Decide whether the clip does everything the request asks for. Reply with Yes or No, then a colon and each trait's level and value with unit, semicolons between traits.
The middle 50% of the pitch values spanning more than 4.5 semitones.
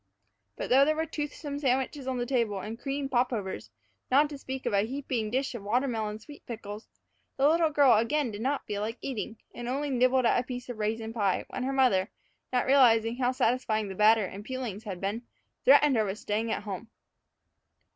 No: average, 3.8 semitones